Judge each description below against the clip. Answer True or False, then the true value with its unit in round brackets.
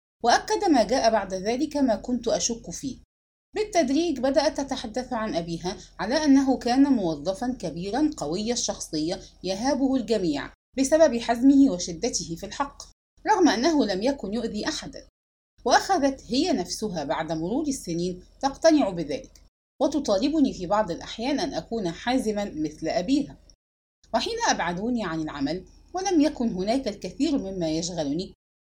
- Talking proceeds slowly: True (130 wpm)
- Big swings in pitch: True (7.2 semitones)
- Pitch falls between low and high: False (245 Hz)